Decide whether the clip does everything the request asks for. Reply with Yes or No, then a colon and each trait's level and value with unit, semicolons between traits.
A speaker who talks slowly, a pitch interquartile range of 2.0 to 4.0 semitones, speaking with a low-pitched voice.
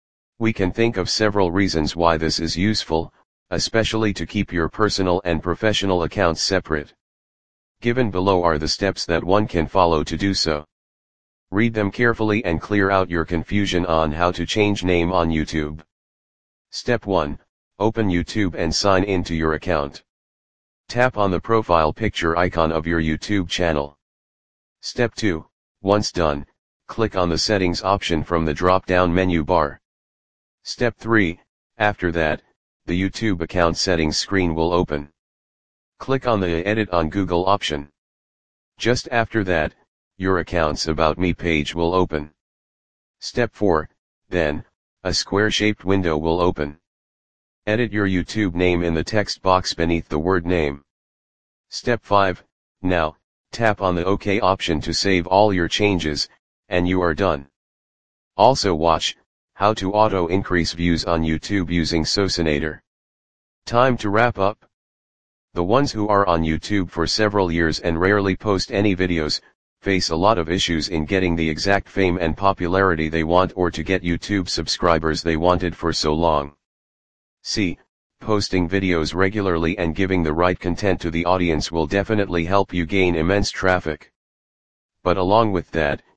No: average, 155 wpm; average, 3.5 semitones; very low, 90 Hz